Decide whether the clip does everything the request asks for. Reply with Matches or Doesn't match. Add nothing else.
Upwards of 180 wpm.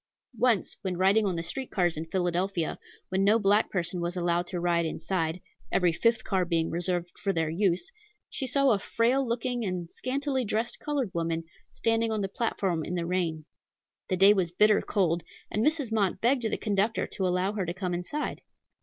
Matches